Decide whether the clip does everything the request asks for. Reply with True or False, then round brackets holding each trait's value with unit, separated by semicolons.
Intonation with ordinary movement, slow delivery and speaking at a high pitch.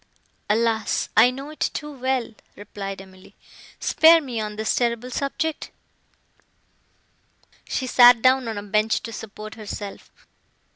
True (3.4 semitones; 130 wpm; 230 Hz)